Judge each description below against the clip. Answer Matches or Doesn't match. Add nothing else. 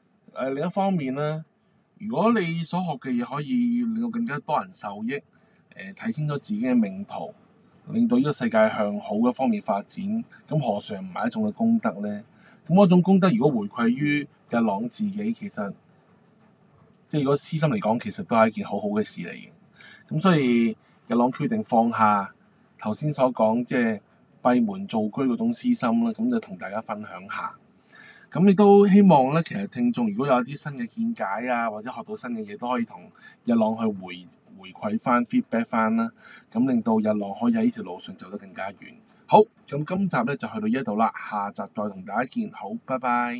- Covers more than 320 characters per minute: Doesn't match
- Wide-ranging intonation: Matches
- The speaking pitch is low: Doesn't match